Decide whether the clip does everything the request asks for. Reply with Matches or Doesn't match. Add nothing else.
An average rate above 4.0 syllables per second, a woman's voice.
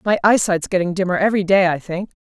Matches